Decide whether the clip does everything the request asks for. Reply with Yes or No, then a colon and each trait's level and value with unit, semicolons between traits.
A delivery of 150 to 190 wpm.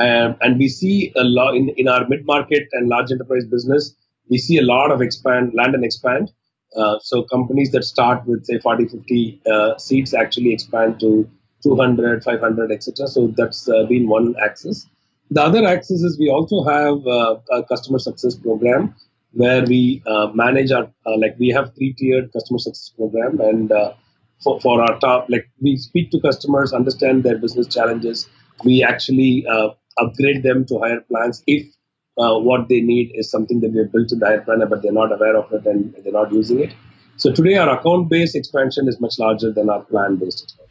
No: average, 200 wpm